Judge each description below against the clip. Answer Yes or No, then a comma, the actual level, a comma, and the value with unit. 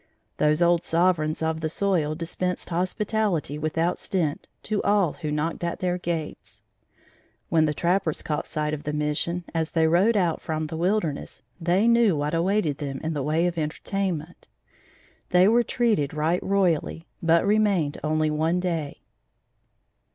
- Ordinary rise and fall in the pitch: Yes, average, 3.1 semitones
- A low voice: No, medium, 165 Hz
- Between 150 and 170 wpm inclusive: Yes, average, 155 wpm